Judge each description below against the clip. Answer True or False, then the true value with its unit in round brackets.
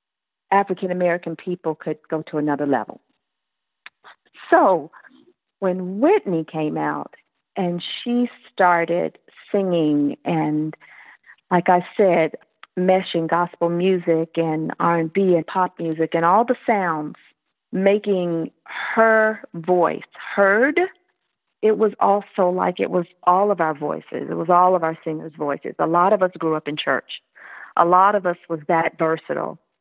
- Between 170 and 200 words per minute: False (145 wpm)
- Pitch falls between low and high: True (175 Hz)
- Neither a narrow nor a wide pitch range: True (3.3 semitones)